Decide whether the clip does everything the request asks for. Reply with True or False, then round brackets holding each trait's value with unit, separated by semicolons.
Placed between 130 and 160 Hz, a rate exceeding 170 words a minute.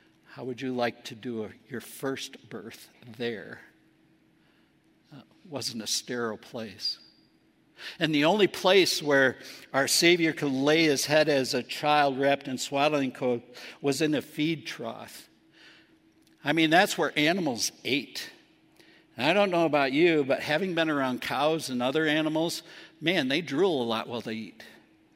False (140 Hz; 160 wpm)